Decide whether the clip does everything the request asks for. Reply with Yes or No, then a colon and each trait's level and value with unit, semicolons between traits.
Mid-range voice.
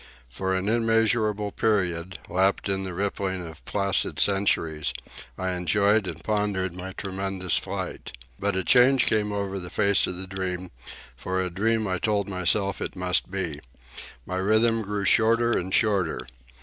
No: very low, 95 Hz